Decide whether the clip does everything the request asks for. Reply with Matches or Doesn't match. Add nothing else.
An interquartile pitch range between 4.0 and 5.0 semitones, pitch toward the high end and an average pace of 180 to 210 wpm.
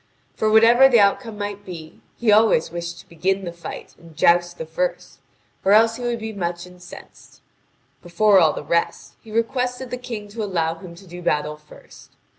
Matches